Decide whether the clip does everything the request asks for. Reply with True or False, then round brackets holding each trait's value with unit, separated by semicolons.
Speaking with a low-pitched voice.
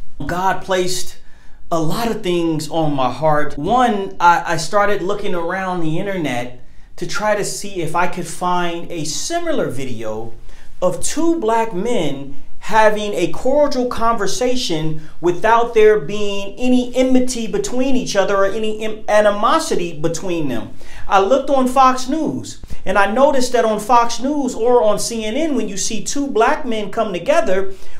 False (200 Hz)